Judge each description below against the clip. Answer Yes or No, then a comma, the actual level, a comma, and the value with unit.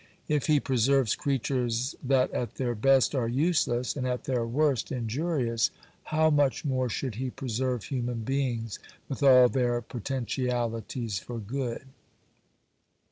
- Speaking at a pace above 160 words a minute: No, slow, 135 wpm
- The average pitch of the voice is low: Yes, low, 125 Hz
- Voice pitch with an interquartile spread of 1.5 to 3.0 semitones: Yes, narrow, 2.4 semitones